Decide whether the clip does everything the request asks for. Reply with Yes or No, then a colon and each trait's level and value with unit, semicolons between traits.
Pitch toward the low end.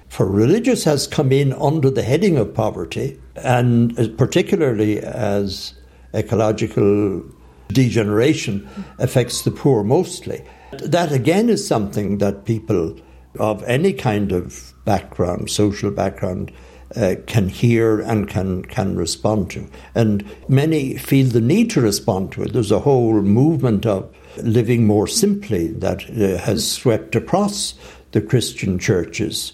Yes: low, 110 Hz